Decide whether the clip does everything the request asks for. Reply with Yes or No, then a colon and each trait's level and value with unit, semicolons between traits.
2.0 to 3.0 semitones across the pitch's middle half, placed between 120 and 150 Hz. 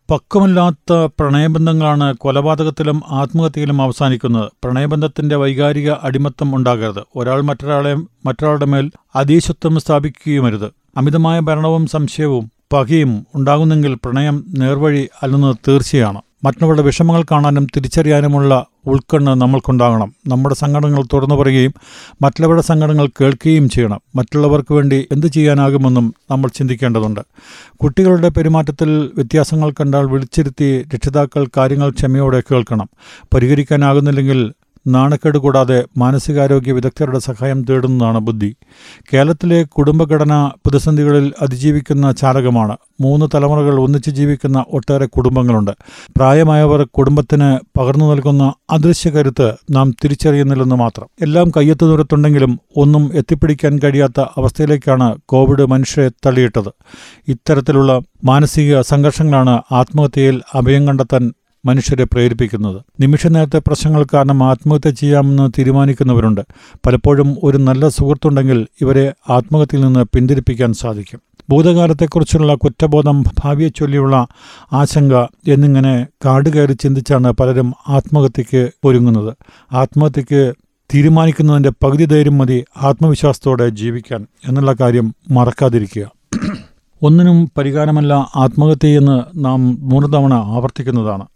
Yes: narrow, 2.4 semitones; medium, 140 Hz